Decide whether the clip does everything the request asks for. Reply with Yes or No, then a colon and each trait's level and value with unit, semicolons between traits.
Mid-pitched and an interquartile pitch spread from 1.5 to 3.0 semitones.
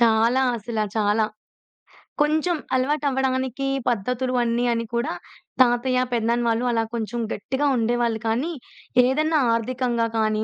No: high, 240 Hz; narrow, 2.4 semitones